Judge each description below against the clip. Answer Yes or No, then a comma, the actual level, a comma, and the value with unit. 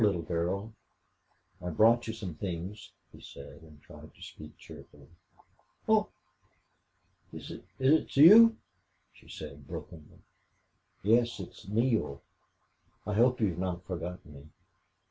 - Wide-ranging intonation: Yes, wide, 5.8 semitones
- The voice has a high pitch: No, very low, 95 Hz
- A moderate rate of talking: No, slow, 120 wpm